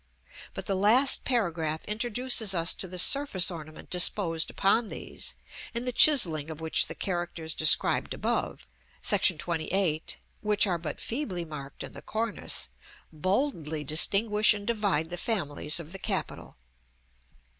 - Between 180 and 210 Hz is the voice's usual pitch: Yes, medium, 185 Hz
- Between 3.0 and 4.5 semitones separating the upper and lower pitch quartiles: No, average, 5.1 semitones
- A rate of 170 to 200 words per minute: No, average, 140 wpm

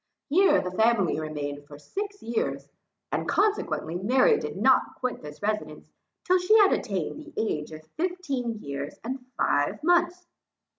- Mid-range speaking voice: No, high, 230 Hz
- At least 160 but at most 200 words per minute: No, average, 150 wpm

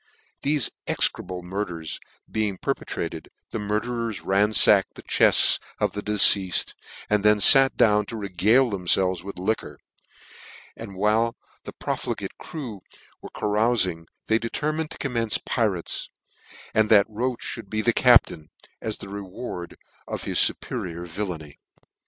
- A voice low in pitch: Yes, low, 105 Hz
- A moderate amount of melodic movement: Yes, average, 3.5 semitones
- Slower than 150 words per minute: Yes, slow, 135 wpm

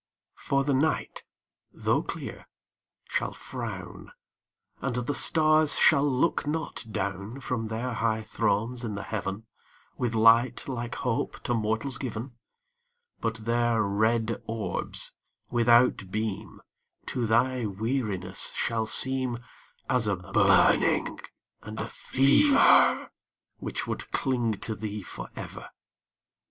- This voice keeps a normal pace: No, slow, 115 wpm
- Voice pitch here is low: Yes, low, 115 Hz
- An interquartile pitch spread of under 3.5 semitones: Yes, average, 2.9 semitones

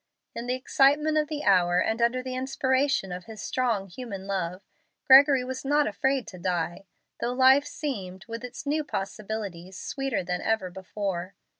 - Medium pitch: No, high, 230 Hz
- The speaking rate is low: No, average, 165 wpm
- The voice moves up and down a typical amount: No, wide, 5.9 semitones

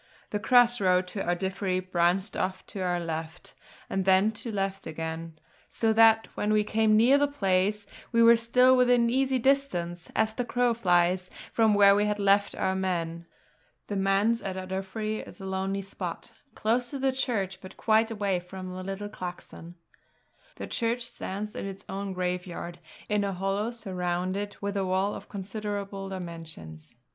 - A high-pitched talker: Yes, high, 195 Hz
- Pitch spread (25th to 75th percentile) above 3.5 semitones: No, average, 3.1 semitones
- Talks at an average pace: Yes, average, 170 wpm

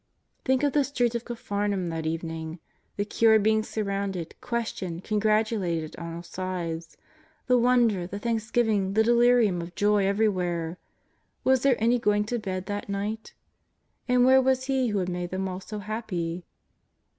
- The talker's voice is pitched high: Yes, high, 205 Hz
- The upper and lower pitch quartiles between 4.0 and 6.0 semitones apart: Yes, average, 4.5 semitones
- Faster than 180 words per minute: No, average, 160 wpm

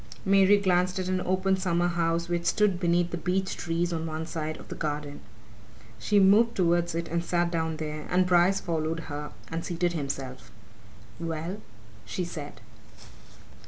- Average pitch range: No, narrow, 2.3 semitones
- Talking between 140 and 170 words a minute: Yes, average, 165 wpm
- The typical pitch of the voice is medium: Yes, medium, 170 Hz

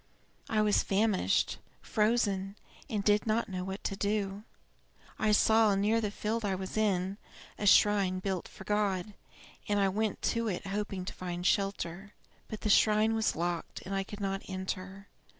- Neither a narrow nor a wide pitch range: No, narrow, 1.9 semitones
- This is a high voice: Yes, high, 200 Hz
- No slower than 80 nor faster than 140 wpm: No, average, 170 wpm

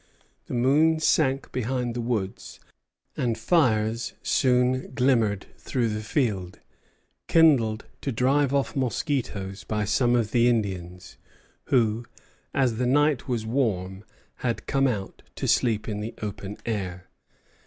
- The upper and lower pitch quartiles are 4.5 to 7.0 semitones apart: No, average, 3.7 semitones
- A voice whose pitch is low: Yes, low, 120 Hz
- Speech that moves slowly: Yes, slow, 130 wpm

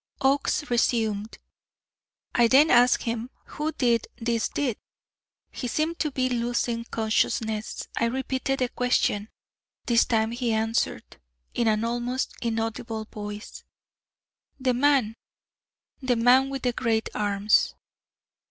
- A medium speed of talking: No, slow, 120 wpm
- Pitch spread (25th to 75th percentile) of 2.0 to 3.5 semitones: Yes, narrow, 2.5 semitones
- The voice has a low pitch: No, high, 235 Hz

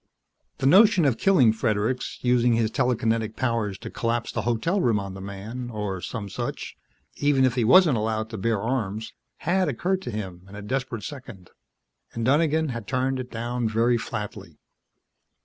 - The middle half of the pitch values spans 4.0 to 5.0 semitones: No, average, 3.4 semitones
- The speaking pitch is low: Yes, low, 115 Hz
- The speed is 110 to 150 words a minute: No, average, 170 wpm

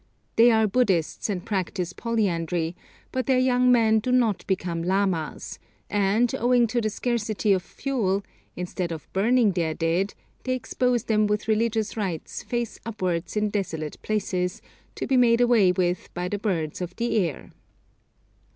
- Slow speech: No, average, 155 wpm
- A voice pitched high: Yes, high, 210 Hz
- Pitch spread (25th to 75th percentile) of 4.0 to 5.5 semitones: Yes, average, 4.5 semitones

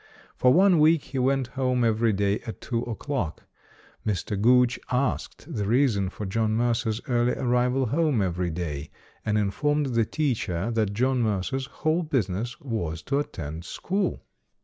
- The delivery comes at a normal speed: Yes, average, 155 wpm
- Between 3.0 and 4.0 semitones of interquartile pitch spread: No, average, 4.8 semitones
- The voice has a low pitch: Yes, low, 120 Hz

